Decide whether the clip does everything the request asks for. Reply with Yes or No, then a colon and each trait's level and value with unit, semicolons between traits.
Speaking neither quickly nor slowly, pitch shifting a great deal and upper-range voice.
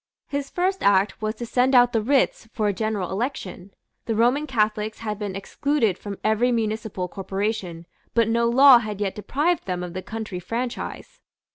No: average, 175 wpm; average, 3.6 semitones; high, 220 Hz